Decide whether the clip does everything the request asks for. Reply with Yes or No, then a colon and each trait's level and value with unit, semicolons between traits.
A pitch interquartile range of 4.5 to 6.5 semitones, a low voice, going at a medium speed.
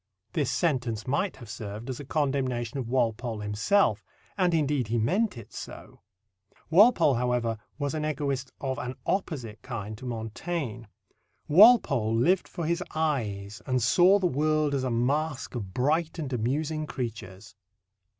Yes: average, 5.1 semitones; low, 130 Hz; average, 150 wpm